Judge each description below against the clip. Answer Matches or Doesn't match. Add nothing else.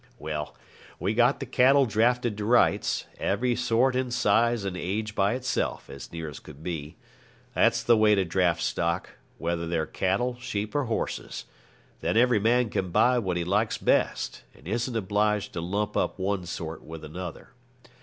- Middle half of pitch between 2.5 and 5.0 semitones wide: Doesn't match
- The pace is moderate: Matches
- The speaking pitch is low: Matches